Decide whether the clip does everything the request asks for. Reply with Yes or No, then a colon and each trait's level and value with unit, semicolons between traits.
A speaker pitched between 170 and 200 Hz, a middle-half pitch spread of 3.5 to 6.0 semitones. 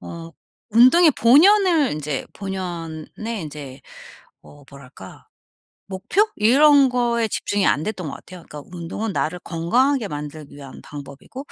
No: medium, 185 Hz; wide, 8.8 semitones